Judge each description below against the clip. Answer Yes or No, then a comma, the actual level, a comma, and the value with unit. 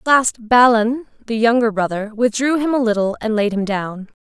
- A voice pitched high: Yes, high, 230 Hz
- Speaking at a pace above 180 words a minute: Yes, average, 200 wpm